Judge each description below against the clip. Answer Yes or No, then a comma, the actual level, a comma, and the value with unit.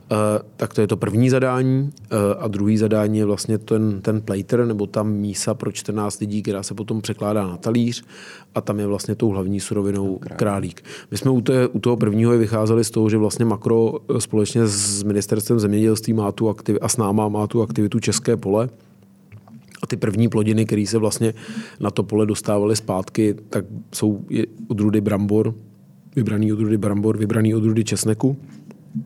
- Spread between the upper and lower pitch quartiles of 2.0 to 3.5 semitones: No, narrow, 1.5 semitones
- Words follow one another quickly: Yes, fast, 175 wpm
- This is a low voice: Yes, low, 110 Hz